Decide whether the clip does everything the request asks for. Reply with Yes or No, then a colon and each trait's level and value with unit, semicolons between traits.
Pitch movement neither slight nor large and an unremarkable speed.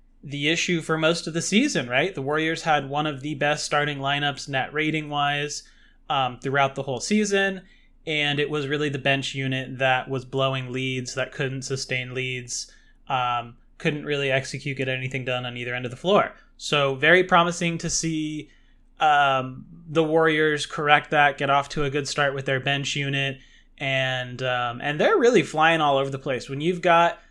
Yes: average, 3.0 semitones; average, 190 wpm